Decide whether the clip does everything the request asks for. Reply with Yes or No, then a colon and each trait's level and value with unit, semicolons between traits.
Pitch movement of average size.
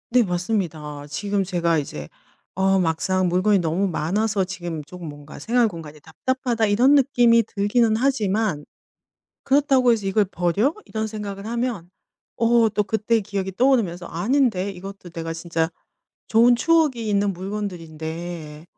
Yes: average, 5.0 semitones